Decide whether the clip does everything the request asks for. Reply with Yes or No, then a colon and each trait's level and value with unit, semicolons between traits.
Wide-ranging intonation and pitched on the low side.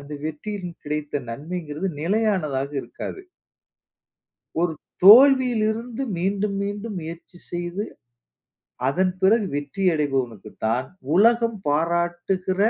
No: wide, 5.8 semitones; medium, 180 Hz